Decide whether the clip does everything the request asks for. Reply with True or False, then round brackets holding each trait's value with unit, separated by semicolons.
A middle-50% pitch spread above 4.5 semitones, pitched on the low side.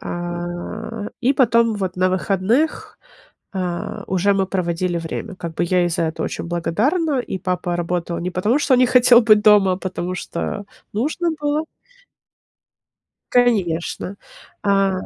False (4.9 semitones; 190 Hz)